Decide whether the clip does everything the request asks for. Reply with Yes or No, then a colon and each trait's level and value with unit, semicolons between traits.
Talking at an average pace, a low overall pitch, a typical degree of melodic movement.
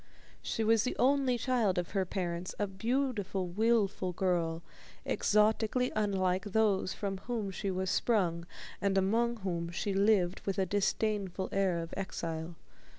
No: average, 145 wpm; high, 195 Hz; average, 3.3 semitones